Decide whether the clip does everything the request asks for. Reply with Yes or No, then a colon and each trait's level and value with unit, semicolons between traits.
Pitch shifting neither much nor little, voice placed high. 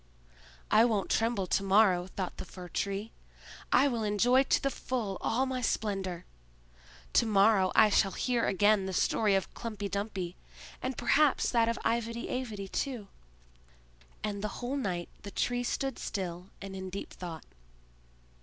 Yes: average, 3.6 semitones; high, 210 Hz